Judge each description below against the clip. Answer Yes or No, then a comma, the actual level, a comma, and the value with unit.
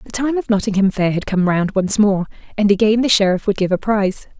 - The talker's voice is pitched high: Yes, high, 205 Hz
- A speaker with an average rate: No, fast, 245 wpm